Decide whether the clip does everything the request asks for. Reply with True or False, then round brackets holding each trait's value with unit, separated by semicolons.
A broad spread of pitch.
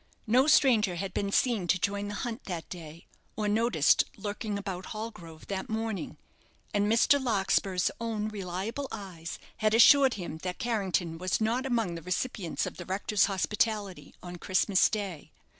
False (3.6 semitones)